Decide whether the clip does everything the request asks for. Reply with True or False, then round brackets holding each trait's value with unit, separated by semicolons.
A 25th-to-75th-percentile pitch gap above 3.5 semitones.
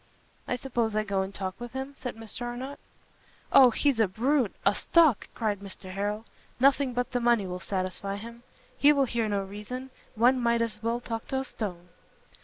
True (3.9 semitones)